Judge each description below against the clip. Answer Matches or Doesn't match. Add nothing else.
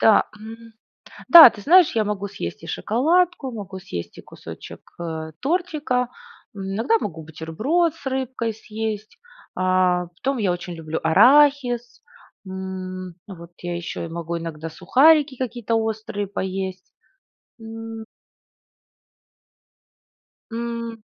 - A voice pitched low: Doesn't match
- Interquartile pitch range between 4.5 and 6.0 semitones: Matches